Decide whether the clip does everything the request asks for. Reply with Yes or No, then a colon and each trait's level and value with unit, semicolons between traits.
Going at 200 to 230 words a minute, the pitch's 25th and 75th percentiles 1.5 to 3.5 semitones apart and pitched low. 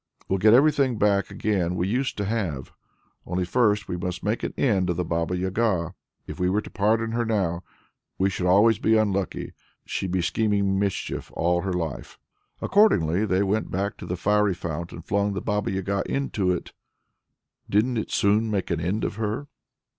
No: average, 185 wpm; average, 3.1 semitones; low, 100 Hz